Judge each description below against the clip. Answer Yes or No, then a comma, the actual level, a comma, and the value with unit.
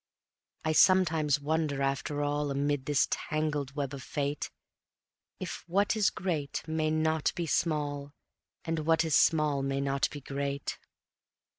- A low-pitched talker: No, medium, 150 Hz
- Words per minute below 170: Yes, average, 140 wpm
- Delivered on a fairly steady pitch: Yes, narrow, 2.1 semitones